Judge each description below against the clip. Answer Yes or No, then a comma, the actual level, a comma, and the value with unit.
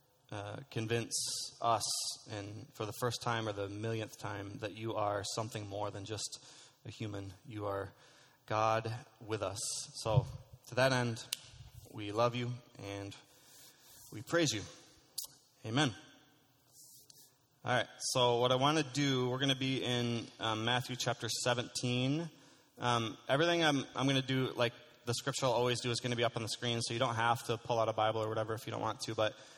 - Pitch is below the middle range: Yes, low, 120 Hz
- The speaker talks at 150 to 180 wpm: No, average, 190 wpm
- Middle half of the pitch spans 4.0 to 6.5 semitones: No, average, 3.0 semitones